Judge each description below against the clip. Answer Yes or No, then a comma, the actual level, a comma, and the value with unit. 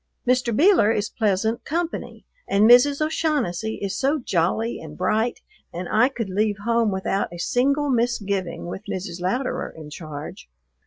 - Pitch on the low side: No, high, 220 Hz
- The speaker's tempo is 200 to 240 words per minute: No, average, 150 wpm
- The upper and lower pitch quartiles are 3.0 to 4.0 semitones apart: No, average, 5.0 semitones